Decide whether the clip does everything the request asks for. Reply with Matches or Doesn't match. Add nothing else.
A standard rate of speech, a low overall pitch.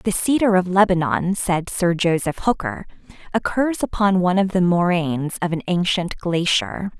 Doesn't match